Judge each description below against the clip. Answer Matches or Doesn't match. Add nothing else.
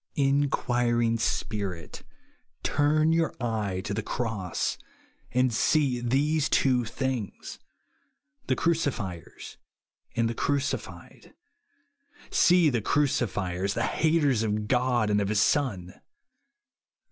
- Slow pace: Matches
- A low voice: Matches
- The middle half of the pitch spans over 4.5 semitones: Matches